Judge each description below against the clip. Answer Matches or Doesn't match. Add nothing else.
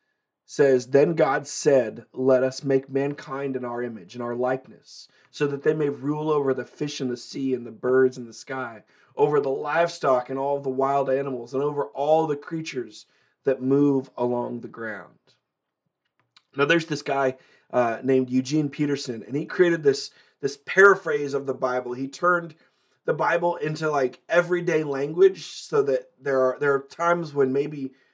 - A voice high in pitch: Doesn't match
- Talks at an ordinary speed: Matches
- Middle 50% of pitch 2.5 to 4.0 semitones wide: Matches